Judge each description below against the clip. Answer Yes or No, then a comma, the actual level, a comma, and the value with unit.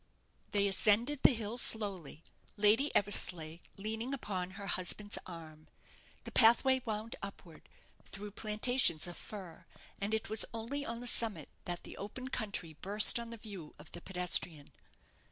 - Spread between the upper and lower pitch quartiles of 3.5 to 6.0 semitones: Yes, average, 4.1 semitones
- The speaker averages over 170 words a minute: No, average, 150 wpm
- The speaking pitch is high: Yes, high, 205 Hz